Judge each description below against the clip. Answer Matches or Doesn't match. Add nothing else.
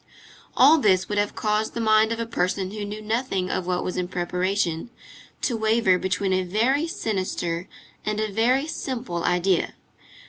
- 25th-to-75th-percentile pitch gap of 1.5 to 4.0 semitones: Matches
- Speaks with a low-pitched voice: Doesn't match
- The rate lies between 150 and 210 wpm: Matches